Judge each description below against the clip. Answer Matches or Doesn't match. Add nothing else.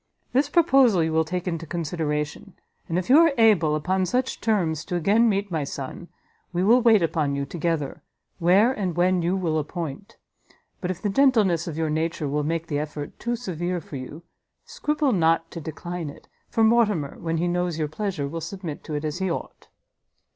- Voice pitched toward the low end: Doesn't match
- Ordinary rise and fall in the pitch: Matches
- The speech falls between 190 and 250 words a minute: Matches